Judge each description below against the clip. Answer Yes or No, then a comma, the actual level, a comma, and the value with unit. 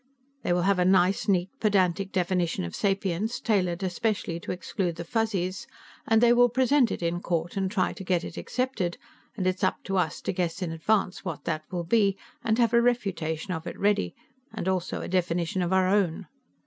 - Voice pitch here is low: No, medium, 185 Hz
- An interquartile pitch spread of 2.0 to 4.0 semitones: Yes, average, 3.0 semitones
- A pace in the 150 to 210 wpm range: Yes, average, 200 wpm